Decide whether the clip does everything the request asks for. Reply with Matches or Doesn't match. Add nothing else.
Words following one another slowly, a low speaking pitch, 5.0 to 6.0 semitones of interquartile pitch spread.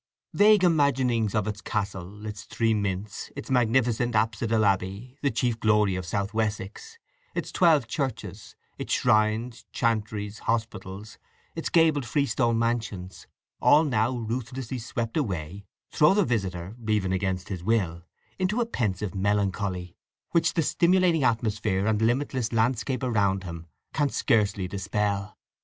Doesn't match